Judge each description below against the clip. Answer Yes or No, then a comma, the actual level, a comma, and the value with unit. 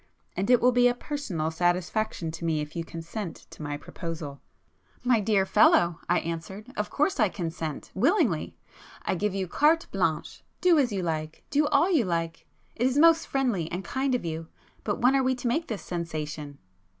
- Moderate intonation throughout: No, wide, 7.5 semitones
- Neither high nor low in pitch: No, high, 195 Hz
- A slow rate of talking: No, average, 185 wpm